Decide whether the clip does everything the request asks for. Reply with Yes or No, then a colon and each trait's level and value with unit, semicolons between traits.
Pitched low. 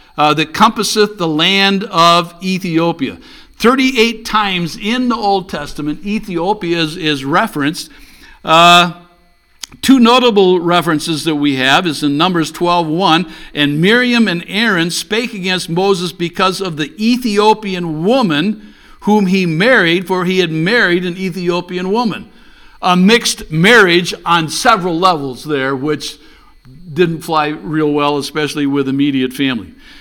No: medium, 175 Hz